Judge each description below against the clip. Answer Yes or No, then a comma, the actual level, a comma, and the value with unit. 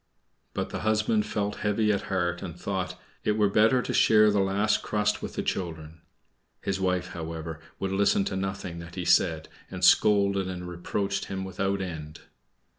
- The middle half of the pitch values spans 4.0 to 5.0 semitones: No, average, 2.8 semitones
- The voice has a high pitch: No, very low, 95 Hz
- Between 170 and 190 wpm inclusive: Yes, average, 175 wpm